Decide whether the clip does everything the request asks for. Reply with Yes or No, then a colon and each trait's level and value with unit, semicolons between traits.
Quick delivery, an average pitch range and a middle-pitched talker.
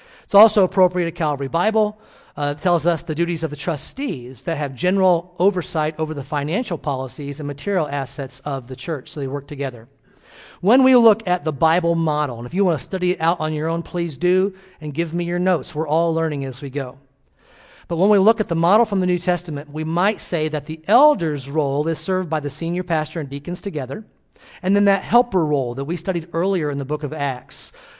Yes: fast, 225 wpm; average, 4.1 semitones; medium, 165 Hz